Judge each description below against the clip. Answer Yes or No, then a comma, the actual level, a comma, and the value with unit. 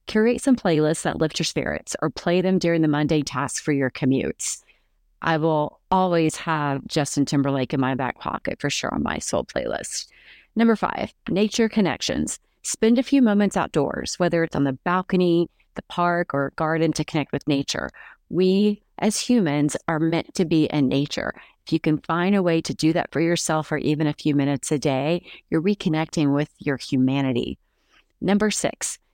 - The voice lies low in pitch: No, medium, 160 Hz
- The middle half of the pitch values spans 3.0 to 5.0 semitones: Yes, average, 4.1 semitones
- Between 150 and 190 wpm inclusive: Yes, average, 185 wpm